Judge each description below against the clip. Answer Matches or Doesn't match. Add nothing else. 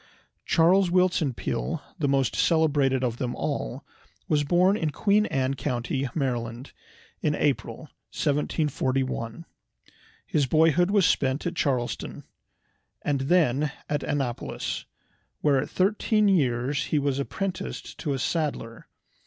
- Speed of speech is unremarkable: Doesn't match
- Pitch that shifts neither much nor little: Matches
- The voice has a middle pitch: Matches